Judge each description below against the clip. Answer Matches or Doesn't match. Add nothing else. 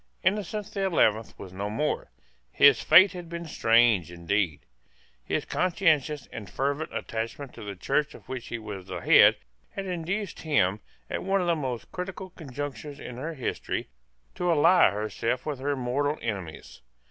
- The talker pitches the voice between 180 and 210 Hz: Doesn't match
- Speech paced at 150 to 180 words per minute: Matches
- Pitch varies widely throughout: Matches